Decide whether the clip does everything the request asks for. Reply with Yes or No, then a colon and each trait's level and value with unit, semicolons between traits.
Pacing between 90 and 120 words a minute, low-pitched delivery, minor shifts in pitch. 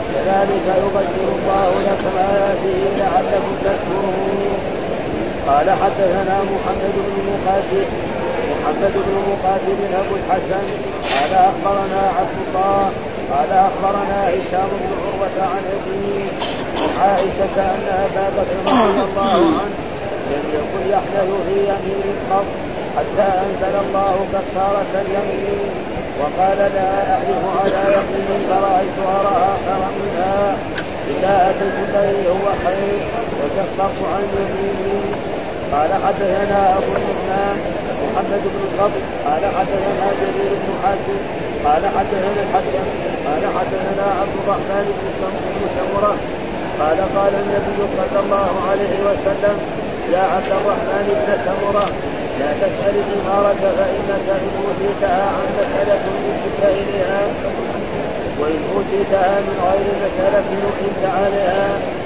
No: average, 105 wpm; high, 195 Hz; narrow, 0.7 semitones